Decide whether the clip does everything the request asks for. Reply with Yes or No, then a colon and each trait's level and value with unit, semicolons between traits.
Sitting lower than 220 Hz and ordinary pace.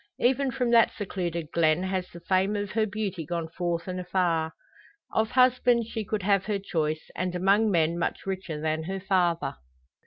Yes: medium, 185 Hz; average, 180 wpm